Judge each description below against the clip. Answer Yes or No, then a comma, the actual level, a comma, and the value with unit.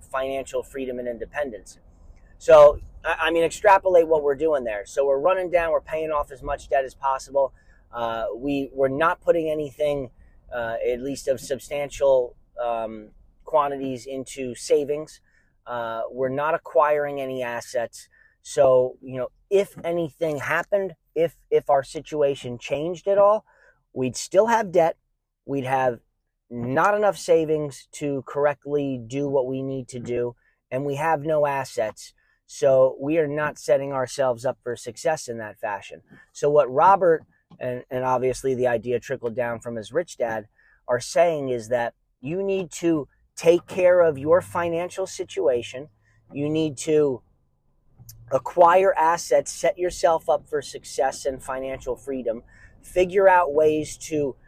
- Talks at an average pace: Yes, average, 150 wpm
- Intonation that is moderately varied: Yes, average, 4.2 semitones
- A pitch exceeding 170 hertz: No, medium, 140 Hz